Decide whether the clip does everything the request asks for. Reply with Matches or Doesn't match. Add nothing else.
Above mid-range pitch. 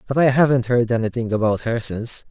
Doesn't match